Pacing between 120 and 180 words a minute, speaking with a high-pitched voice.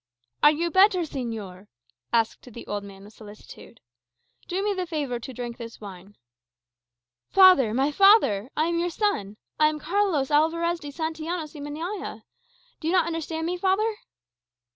Yes: average, 165 wpm; very high, 305 Hz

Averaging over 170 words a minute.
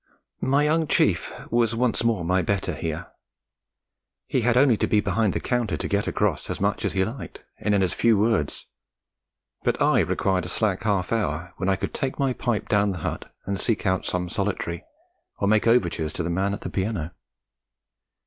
Yes: average, 195 wpm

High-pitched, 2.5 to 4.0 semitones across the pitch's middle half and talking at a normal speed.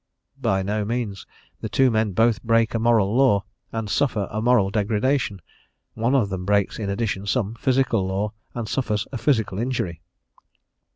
No: low, 110 Hz; average, 3.0 semitones; average, 165 wpm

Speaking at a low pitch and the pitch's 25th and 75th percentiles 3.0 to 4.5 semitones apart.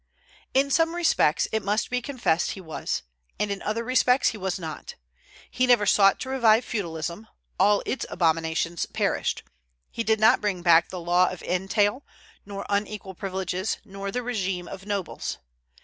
No: high, 200 Hz; average, 3.9 semitones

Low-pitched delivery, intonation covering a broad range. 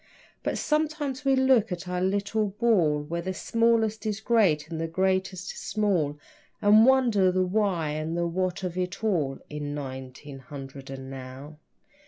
No: medium, 185 Hz; wide, 6.4 semitones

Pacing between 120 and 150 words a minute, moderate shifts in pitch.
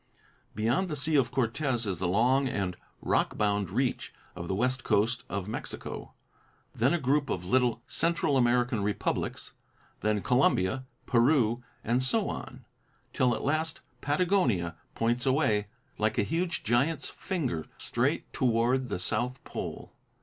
Yes: average, 140 wpm; average, 4.4 semitones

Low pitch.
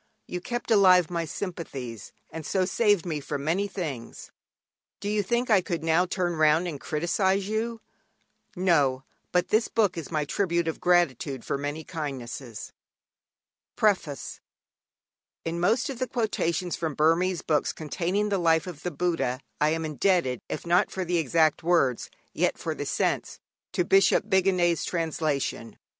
No: medium, 170 Hz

